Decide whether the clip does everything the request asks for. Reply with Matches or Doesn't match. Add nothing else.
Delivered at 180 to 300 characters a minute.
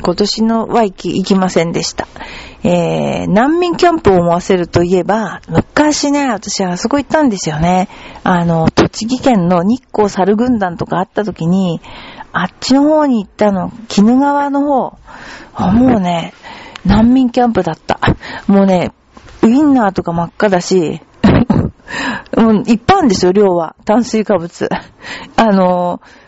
Matches